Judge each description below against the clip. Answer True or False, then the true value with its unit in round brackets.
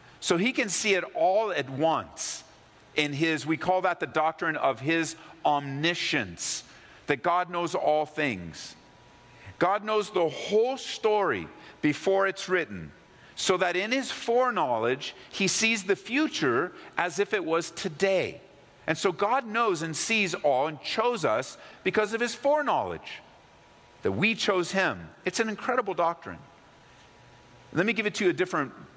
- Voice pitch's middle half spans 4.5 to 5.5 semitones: True (5.1 semitones)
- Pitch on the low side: False (185 Hz)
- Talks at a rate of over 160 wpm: False (155 wpm)